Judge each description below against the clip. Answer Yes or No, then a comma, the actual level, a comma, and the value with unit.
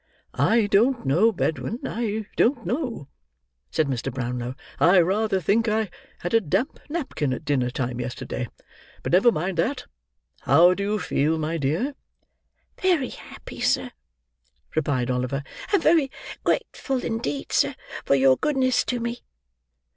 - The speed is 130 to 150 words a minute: Yes, average, 140 wpm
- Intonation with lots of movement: Yes, wide, 8.9 semitones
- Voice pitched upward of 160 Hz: Yes, high, 190 Hz